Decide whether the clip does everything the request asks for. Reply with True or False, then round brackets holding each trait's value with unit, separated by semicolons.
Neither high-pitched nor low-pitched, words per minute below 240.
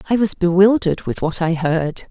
True (180 Hz; 200 wpm)